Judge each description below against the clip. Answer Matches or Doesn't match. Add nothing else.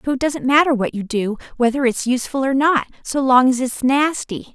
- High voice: Matches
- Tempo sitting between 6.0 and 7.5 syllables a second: Doesn't match